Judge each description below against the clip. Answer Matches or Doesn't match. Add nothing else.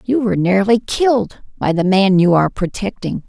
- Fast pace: Doesn't match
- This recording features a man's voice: Doesn't match